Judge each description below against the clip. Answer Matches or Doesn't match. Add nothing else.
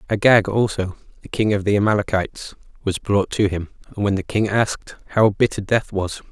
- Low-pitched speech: Matches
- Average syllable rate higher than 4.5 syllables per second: Matches